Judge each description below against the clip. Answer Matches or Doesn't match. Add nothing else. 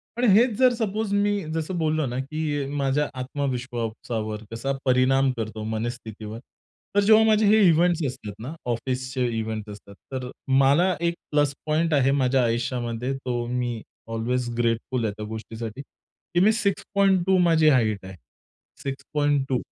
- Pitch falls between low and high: Doesn't match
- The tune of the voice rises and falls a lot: Matches